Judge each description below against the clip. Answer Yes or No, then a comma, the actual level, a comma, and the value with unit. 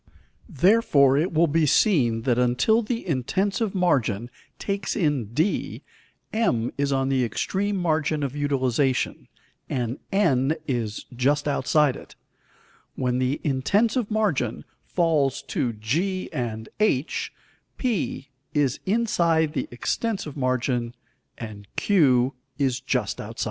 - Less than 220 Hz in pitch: Yes, medium, 140 Hz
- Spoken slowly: Yes, slow, 120 wpm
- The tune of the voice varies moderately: No, wide, 6.5 semitones